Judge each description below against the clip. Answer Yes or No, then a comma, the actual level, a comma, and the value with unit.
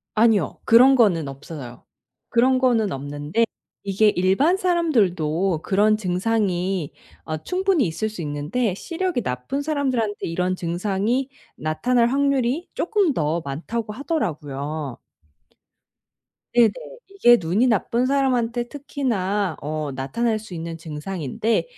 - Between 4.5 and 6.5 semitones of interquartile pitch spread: No, wide, 7.5 semitones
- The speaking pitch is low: No, high, 210 Hz